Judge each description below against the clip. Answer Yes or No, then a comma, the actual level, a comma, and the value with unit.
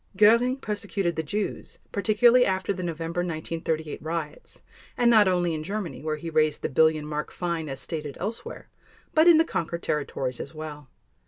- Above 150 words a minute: Yes, average, 170 wpm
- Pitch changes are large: No, average, 5.0 semitones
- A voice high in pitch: No, medium, 170 Hz